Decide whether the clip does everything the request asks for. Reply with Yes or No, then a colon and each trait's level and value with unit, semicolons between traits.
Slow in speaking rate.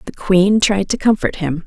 No: fast, 215 wpm